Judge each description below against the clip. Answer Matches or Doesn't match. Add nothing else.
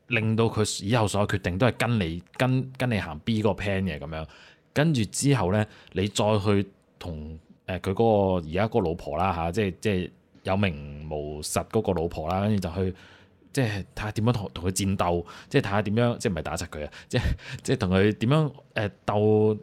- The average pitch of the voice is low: Matches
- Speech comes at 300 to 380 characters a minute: Matches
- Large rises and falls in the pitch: Doesn't match